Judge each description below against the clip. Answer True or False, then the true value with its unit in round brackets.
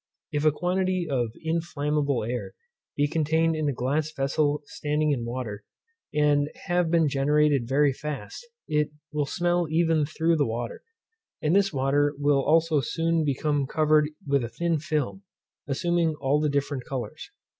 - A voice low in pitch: False (150 Hz)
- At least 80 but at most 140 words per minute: False (155 wpm)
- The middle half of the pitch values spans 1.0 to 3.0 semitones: True (2.6 semitones)